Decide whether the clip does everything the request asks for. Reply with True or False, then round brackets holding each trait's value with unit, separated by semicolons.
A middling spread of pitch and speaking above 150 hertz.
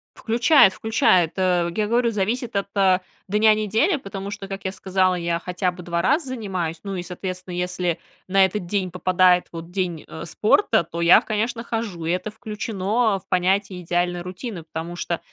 True (3.2 semitones; 190 Hz)